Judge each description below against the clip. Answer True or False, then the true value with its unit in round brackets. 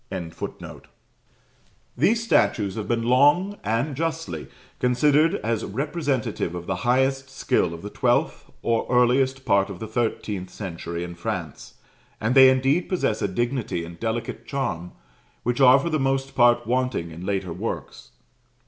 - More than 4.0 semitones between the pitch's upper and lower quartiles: True (5.5 semitones)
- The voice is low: True (120 Hz)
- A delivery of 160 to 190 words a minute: False (150 wpm)